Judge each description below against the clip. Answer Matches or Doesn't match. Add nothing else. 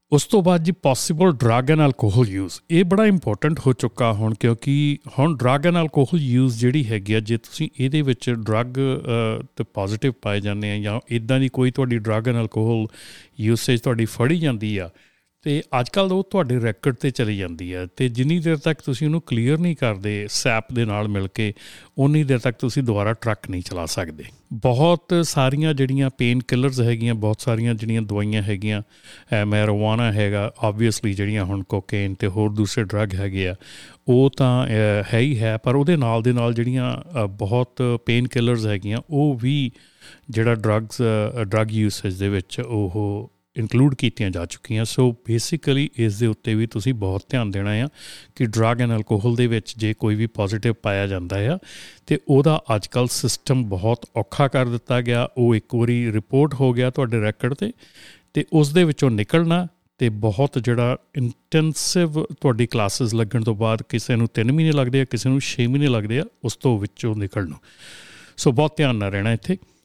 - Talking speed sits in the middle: Doesn't match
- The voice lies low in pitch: Matches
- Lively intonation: Doesn't match